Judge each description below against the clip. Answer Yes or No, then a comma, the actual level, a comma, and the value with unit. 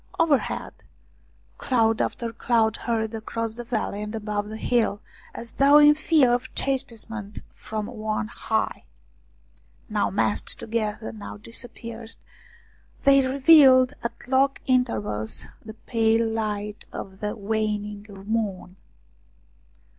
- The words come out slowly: Yes, slow, 115 wpm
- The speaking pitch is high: Yes, high, 225 Hz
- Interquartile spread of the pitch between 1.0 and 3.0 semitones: Yes, narrow, 2.6 semitones